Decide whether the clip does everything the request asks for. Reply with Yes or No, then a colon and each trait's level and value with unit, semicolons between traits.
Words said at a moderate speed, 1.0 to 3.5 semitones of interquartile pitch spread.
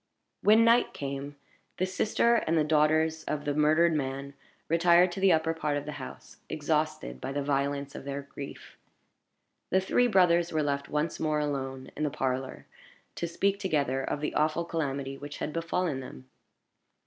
Yes: average, 170 wpm; average, 3.2 semitones